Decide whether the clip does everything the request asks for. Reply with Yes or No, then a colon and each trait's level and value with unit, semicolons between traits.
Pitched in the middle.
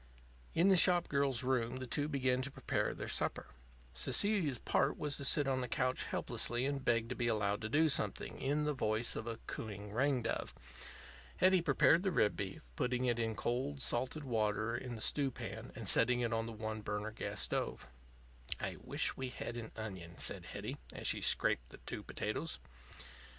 No: low, 125 Hz